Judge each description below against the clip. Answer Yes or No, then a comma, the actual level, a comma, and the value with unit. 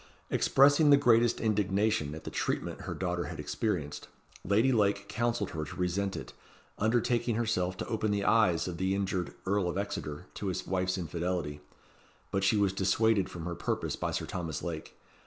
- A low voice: Yes, low, 100 Hz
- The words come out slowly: No, average, 175 wpm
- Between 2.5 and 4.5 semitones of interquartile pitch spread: Yes, average, 3.7 semitones